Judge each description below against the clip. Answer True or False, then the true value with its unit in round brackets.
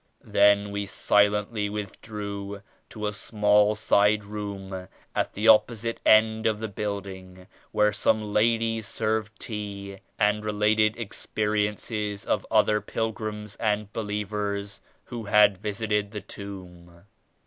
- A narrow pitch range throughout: True (1.0 semitones)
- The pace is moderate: False (120 wpm)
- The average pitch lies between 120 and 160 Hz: False (105 Hz)